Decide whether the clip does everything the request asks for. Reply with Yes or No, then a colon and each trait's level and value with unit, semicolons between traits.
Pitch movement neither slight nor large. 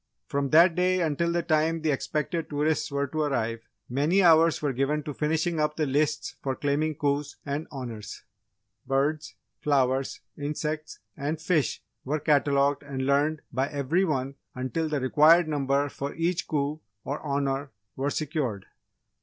No: narrow, 2.1 semitones